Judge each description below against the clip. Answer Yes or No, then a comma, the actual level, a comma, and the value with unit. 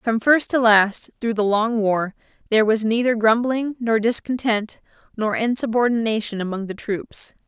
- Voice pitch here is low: No, high, 225 Hz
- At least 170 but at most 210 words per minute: No, average, 155 wpm